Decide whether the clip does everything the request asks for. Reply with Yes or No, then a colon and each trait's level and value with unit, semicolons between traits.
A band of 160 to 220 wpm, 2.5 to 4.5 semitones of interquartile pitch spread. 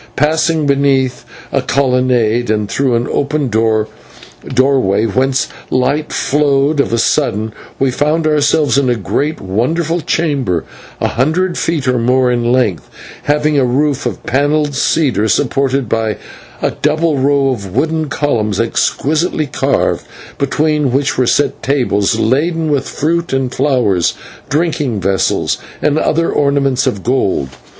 No: average, 140 wpm; average, 3.7 semitones